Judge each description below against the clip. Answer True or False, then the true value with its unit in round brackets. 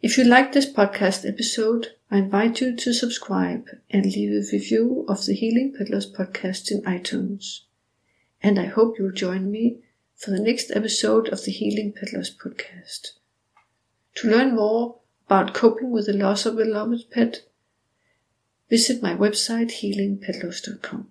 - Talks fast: False (150 wpm)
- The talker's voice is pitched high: True (210 Hz)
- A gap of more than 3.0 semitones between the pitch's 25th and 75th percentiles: True (3.5 semitones)